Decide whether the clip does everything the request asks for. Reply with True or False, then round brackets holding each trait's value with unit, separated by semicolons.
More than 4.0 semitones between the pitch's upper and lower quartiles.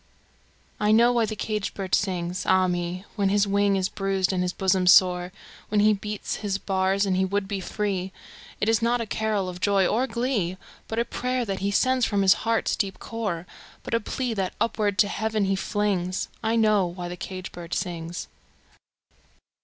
False (2.7 semitones)